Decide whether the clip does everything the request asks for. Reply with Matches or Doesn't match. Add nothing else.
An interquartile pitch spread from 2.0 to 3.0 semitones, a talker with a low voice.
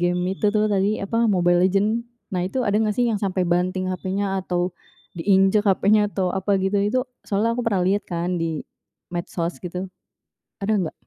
Doesn't match